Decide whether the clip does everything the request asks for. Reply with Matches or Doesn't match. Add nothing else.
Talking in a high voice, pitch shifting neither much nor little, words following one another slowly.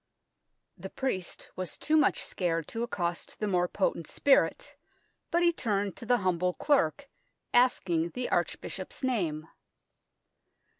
Doesn't match